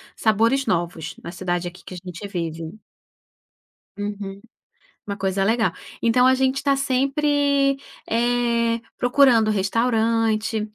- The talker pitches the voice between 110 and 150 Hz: No, high, 225 Hz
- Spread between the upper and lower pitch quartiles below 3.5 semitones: No, average, 4.6 semitones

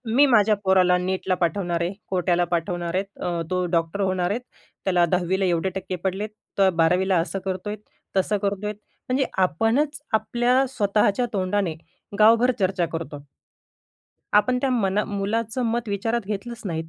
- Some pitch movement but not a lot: Yes, average, 3.2 semitones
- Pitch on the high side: Yes, high, 195 Hz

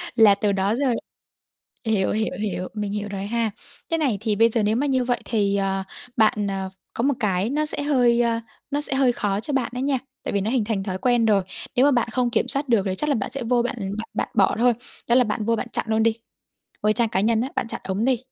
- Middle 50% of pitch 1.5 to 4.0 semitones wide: Yes, average, 3.4 semitones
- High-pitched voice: Yes, high, 225 Hz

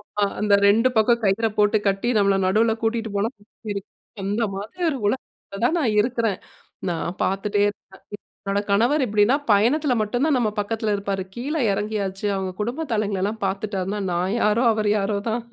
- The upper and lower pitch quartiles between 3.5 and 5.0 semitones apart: No, narrow, 2.5 semitones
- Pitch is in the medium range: No, high, 210 Hz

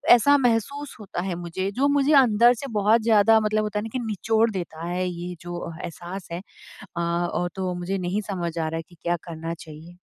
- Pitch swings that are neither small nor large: Yes, average, 4.4 semitones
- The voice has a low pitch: No, high, 190 Hz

